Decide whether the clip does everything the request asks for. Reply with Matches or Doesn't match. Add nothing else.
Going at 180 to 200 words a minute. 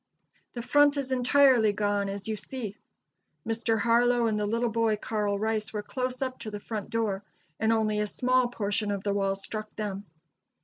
Matches